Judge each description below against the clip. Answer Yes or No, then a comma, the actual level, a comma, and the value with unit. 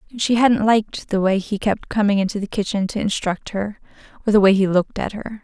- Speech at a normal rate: No, fast, 245 wpm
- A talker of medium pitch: No, high, 205 Hz